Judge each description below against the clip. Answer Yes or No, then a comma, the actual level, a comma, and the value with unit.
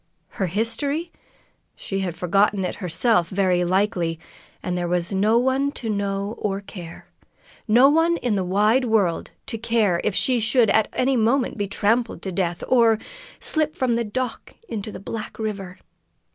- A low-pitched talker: No, high, 210 Hz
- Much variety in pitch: No, average, 3.9 semitones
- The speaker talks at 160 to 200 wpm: Yes, average, 165 wpm